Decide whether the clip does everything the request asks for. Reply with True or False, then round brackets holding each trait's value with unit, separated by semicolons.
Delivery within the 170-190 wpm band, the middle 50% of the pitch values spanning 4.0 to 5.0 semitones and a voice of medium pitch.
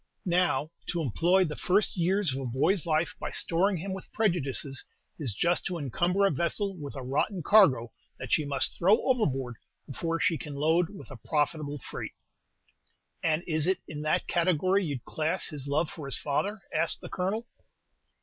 True (180 wpm; 4.5 semitones; 165 Hz)